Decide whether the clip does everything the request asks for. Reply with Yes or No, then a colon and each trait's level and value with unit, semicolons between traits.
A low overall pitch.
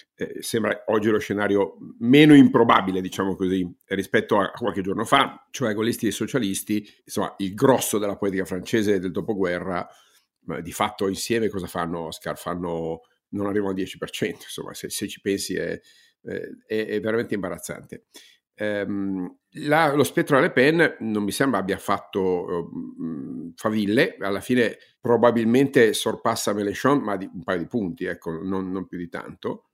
Yes: low, 100 Hz